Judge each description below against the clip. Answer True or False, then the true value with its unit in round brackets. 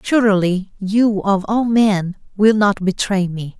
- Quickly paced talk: False (150 wpm)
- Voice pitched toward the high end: True (200 Hz)